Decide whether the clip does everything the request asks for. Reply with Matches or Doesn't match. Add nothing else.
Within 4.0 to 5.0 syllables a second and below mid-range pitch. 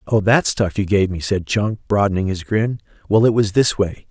Matches